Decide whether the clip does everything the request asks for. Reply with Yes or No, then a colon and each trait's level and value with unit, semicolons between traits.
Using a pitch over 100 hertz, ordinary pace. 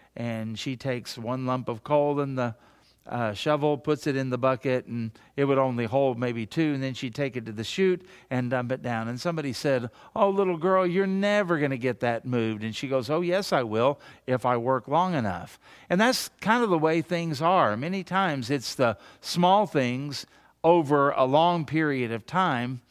No: low, 135 Hz; fast, 210 wpm